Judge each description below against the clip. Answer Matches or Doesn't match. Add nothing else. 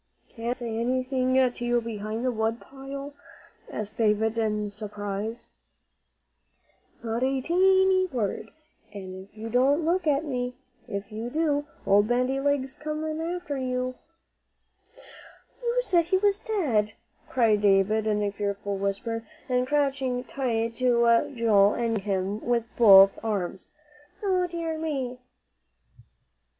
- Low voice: Doesn't match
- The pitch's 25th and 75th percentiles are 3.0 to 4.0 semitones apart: Doesn't match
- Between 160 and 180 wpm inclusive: Doesn't match